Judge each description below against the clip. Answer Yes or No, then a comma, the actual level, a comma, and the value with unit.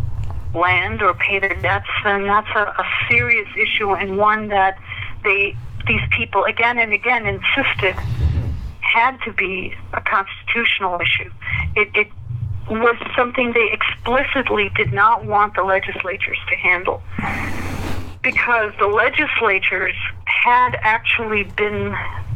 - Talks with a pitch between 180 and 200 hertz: Yes, high, 190 Hz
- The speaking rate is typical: No, slow, 125 wpm